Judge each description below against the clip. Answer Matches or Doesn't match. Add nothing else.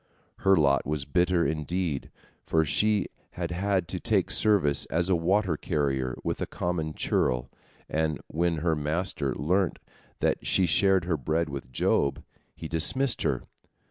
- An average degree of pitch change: Matches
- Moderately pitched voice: Doesn't match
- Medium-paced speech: Matches